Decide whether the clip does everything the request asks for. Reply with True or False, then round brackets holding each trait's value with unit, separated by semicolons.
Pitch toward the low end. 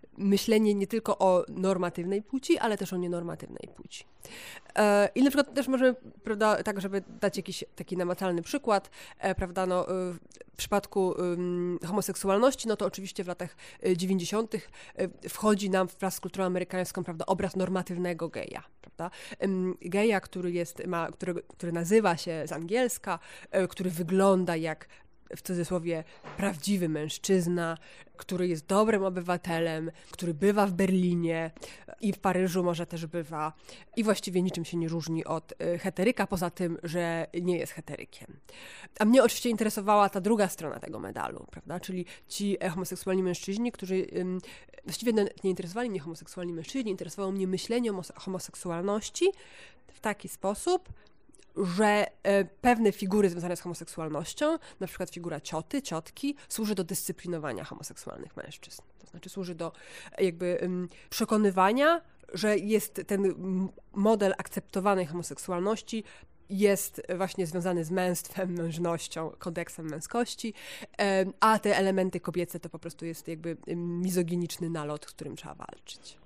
False (185 Hz)